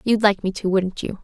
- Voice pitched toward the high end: Yes, high, 200 Hz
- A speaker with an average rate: No, fast, 290 wpm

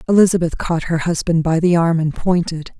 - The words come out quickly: No, average, 195 wpm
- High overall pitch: No, medium, 170 Hz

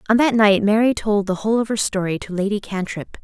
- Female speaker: Yes, female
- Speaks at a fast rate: Yes, fast, 240 wpm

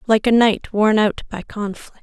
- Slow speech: No, fast, 205 wpm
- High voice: Yes, high, 215 Hz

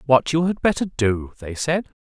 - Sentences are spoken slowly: No, fast, 205 wpm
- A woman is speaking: No, male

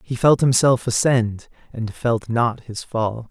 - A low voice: Yes, low, 120 Hz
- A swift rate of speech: No, average, 165 wpm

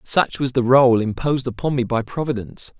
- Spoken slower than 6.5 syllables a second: Yes, 5.6 syllables/s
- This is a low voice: Yes, low, 125 Hz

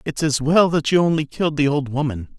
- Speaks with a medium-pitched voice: Yes, medium, 145 Hz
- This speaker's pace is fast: Yes, fast, 250 wpm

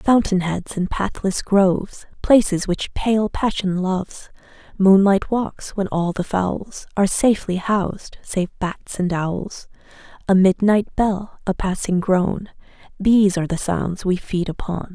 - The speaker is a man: No, female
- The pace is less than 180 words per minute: Yes, average, 145 wpm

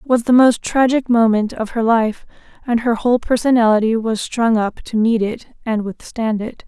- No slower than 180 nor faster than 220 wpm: Yes, average, 200 wpm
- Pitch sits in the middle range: No, high, 230 Hz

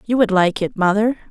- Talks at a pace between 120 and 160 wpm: No, fast, 230 wpm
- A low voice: No, high, 210 Hz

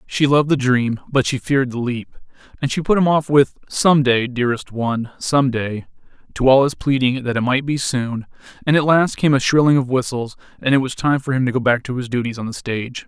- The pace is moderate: No, fast, 245 wpm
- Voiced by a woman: No, male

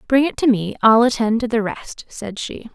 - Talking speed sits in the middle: No, fast, 240 wpm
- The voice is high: Yes, high, 230 Hz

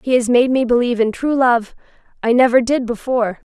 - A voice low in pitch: No, high, 240 Hz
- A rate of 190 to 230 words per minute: Yes, fast, 205 wpm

